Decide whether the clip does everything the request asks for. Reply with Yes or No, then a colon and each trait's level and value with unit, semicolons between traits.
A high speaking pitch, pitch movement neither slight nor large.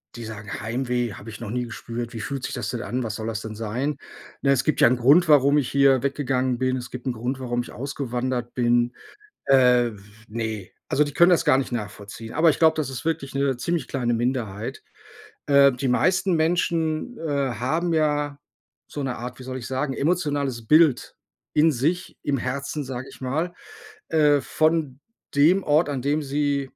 No: low, 135 Hz; average, 3.4 semitones